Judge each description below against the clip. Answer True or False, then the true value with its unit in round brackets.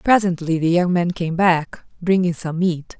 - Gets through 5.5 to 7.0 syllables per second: False (4.4 syllables/s)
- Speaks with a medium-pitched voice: True (175 Hz)